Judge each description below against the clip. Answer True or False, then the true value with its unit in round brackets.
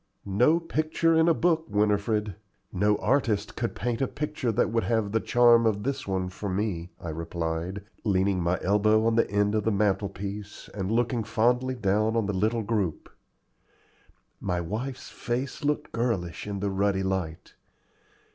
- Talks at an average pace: True (165 wpm)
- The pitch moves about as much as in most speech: True (3.5 semitones)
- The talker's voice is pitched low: True (105 Hz)